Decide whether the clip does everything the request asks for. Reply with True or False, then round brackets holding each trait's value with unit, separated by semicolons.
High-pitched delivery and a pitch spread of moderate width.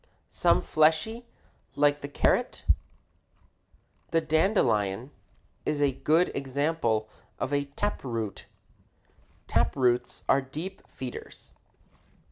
False (140 Hz; 4.0 semitones)